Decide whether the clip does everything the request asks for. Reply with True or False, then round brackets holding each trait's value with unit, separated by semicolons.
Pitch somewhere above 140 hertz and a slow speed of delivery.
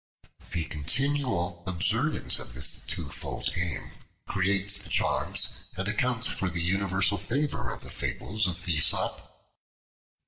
False (95 Hz; 125 wpm)